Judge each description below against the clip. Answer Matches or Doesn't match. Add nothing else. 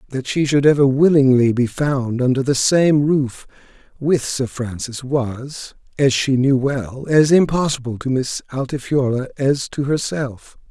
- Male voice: Matches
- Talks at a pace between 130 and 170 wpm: Matches